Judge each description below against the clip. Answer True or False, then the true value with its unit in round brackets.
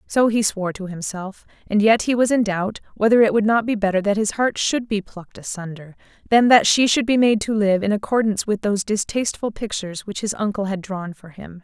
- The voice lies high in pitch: True (210 Hz)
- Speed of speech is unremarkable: False (225 wpm)